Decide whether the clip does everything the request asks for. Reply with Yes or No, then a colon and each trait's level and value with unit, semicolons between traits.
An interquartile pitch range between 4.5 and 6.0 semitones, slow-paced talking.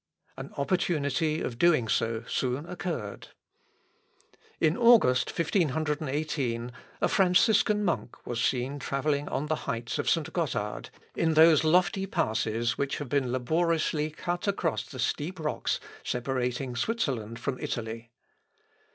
Yes: average, 5.2 semitones; slow, 125 wpm